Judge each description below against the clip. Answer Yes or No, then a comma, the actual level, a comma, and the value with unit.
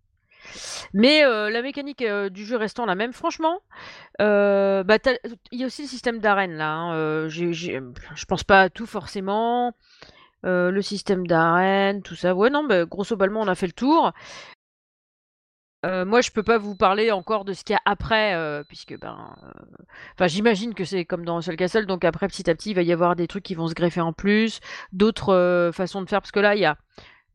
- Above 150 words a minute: Yes, average, 215 wpm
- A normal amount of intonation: Yes, average, 3.9 semitones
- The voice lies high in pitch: Yes, high, 195 Hz